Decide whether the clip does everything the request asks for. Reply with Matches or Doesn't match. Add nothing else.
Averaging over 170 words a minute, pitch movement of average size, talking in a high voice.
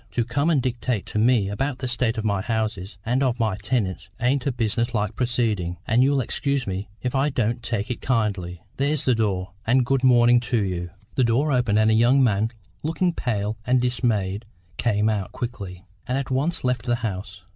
Doesn't match